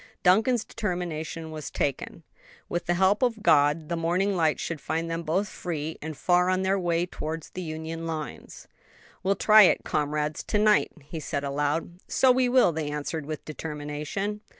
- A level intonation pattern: No, average, 3.7 semitones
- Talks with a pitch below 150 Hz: No, medium, 165 Hz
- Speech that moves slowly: No, average, 175 wpm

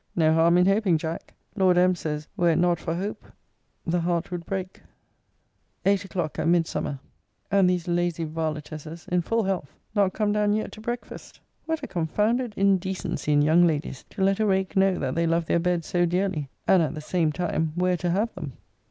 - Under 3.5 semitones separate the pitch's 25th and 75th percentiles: Yes, average, 3.1 semitones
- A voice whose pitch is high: No, medium, 175 Hz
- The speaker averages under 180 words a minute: No, average, 195 wpm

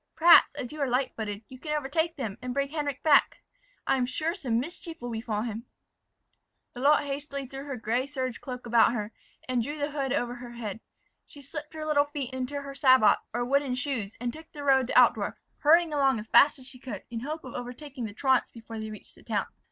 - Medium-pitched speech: No, very high, 260 Hz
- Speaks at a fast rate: Yes, fast, 220 wpm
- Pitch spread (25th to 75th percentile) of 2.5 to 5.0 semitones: Yes, average, 3.2 semitones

